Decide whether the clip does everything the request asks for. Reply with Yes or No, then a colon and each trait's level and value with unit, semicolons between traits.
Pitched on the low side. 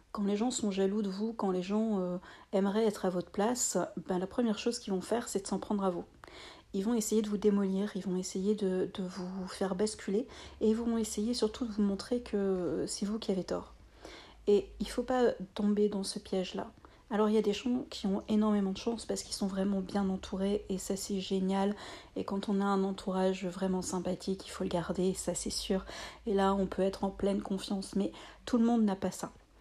No: high, 200 Hz